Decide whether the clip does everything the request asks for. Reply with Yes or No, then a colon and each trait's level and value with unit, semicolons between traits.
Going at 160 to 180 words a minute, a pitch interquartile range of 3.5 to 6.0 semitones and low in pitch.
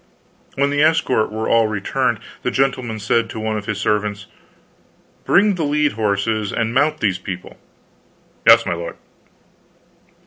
No: average, 145 wpm; average, 4.7 semitones; low, 110 Hz